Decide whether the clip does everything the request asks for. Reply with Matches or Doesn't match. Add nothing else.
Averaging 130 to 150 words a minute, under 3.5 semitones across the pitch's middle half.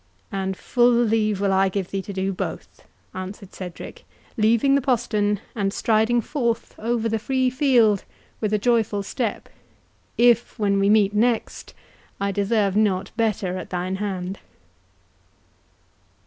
Matches